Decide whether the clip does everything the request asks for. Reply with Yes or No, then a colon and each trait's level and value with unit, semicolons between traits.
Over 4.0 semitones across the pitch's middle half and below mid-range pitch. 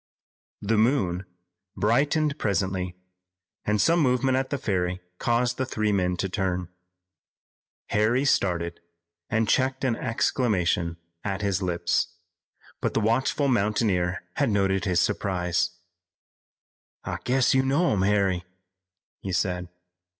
Yes: wide, 5.6 semitones; low, 105 Hz